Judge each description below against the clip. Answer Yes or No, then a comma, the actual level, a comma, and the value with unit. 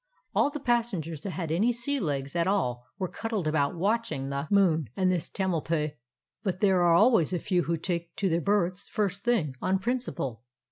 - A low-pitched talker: No, medium, 180 Hz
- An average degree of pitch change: Yes, average, 4.5 semitones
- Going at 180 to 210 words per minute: Yes, average, 195 wpm